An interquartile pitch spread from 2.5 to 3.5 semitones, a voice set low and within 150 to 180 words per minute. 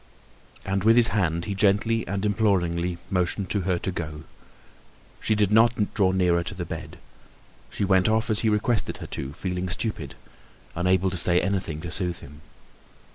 Yes: average, 3.1 semitones; very low, 95 Hz; average, 175 wpm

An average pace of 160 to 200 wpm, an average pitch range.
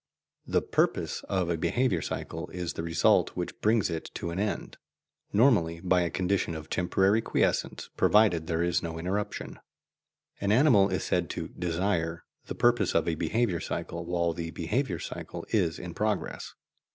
Yes: average, 165 wpm; average, 3.7 semitones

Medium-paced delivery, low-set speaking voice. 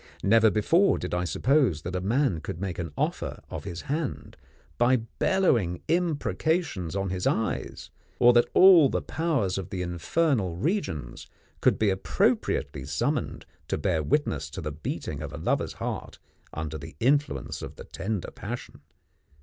Yes: average, 160 wpm; low, 100 Hz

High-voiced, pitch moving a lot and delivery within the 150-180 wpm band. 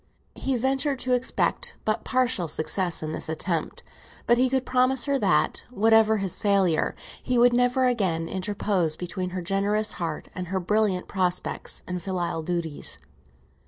Yes: high, 200 Hz; wide, 5.7 semitones; average, 155 wpm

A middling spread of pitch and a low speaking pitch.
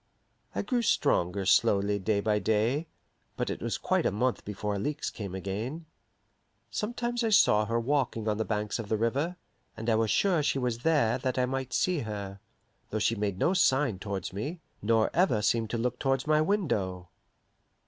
No: wide, 5.8 semitones; low, 115 Hz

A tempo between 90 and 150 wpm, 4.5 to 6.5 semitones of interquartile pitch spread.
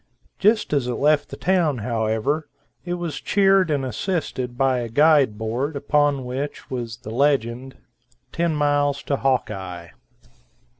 No: average, 140 wpm; average, 3.9 semitones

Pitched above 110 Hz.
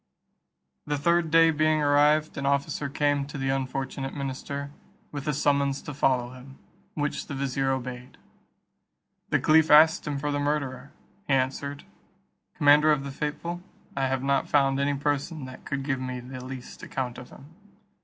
Yes: medium, 140 Hz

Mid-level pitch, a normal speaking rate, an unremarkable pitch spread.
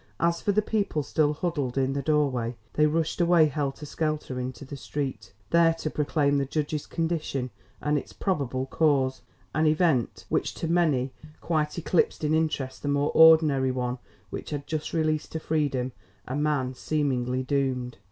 Yes: medium, 150 Hz; average, 165 wpm; average, 3.1 semitones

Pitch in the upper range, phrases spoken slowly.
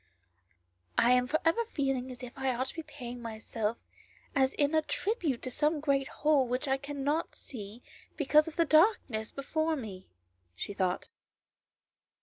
No: very high, 270 Hz; average, 160 wpm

